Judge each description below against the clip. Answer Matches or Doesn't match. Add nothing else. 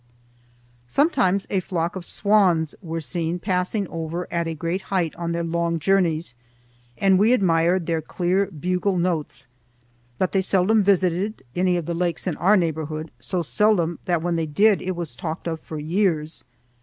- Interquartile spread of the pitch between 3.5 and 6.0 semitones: Doesn't match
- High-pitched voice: Doesn't match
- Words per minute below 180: Matches